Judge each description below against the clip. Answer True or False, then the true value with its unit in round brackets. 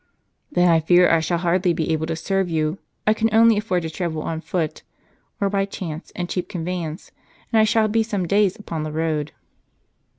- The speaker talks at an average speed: False (210 wpm)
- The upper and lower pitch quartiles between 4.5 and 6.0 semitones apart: False (3.8 semitones)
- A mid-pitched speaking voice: True (175 Hz)